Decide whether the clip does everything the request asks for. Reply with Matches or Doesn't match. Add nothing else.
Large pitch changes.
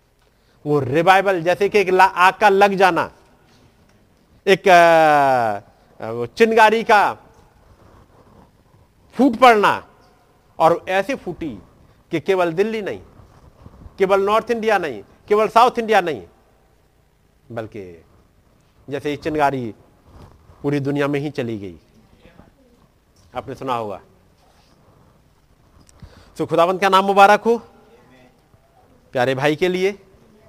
Matches